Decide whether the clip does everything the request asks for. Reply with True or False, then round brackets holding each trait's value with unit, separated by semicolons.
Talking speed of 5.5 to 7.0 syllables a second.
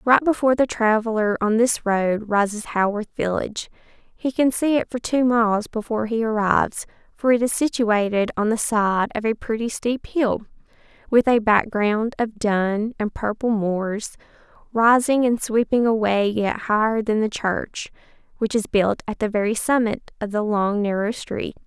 False (4.6 syllables/s)